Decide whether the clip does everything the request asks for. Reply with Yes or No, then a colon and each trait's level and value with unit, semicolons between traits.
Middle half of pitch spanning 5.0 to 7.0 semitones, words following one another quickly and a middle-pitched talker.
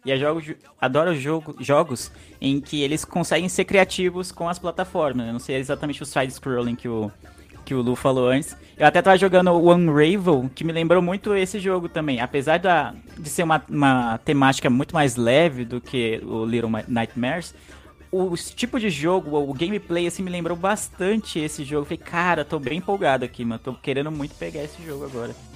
Yes: average, 5.3 semitones; fast, 190 wpm; medium, 150 Hz